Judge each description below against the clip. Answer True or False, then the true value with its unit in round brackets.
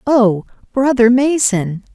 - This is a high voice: True (235 Hz)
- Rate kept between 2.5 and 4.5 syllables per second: True (3.4 syllables/s)